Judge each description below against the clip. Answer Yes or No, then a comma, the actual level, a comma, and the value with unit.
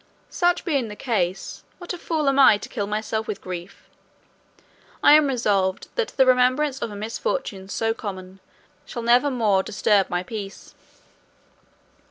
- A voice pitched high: Yes, high, 225 Hz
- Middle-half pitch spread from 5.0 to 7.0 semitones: Yes, wide, 5.5 semitones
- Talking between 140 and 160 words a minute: Yes, average, 155 wpm